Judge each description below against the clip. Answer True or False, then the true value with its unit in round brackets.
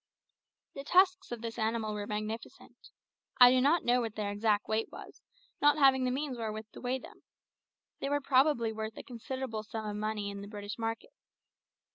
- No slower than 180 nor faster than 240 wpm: True (185 wpm)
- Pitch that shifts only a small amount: False (3.5 semitones)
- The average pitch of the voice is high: True (230 Hz)